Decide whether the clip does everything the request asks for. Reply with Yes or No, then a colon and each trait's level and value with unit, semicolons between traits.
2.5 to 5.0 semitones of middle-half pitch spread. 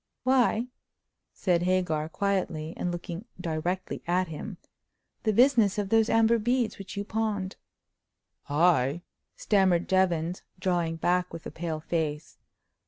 Yes: average, 3.8 semitones